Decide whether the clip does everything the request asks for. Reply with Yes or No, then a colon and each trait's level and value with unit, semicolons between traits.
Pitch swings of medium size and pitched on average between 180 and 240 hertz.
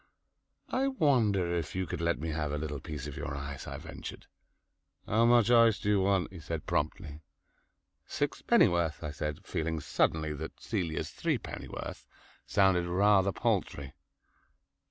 No: average, 4.8 semitones; very low, 85 Hz